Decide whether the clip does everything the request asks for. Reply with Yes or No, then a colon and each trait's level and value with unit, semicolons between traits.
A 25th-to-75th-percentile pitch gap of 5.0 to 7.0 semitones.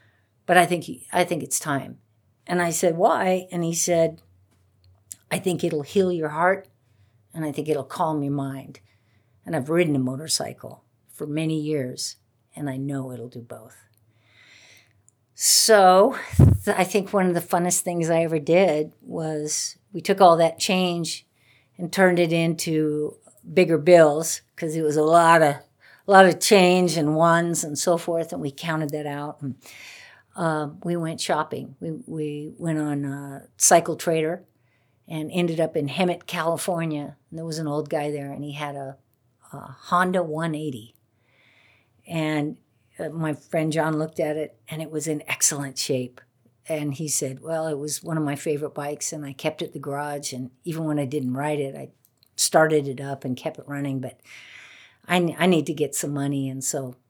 No: average, 3.6 semitones